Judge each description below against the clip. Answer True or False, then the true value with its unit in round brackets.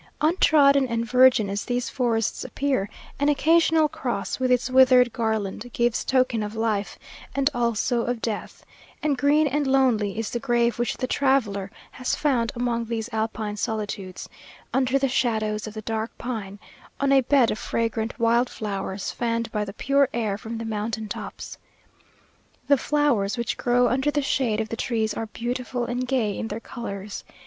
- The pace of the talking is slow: False (170 wpm)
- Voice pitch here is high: True (235 Hz)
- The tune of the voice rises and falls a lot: False (3.1 semitones)